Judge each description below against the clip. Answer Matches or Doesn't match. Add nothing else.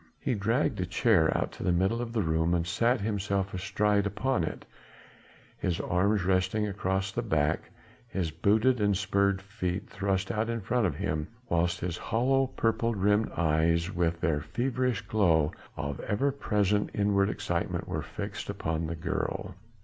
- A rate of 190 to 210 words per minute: Doesn't match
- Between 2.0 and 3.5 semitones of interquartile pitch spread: Doesn't match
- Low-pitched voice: Matches